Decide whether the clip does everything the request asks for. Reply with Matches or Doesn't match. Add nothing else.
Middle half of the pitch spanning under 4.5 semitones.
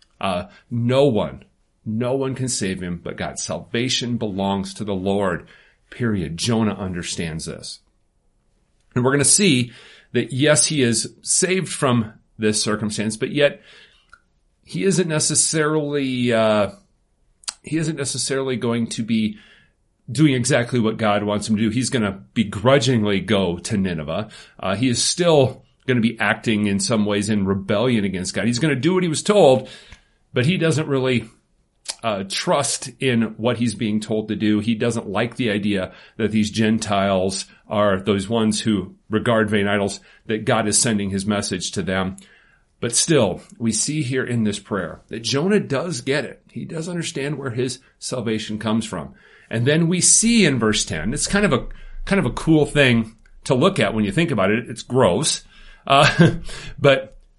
Doesn't match